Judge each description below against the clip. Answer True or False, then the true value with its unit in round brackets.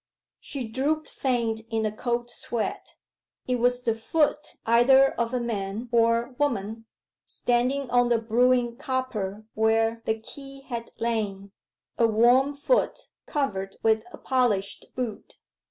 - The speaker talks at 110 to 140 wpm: True (135 wpm)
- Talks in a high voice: True (235 Hz)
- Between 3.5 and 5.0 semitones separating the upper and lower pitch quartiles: False (2.6 semitones)